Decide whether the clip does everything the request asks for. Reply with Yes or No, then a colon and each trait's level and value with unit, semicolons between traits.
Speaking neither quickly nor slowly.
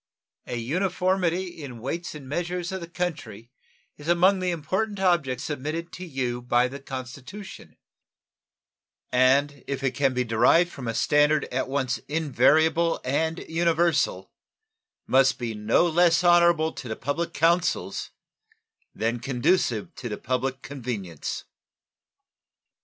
No: slow, 130 wpm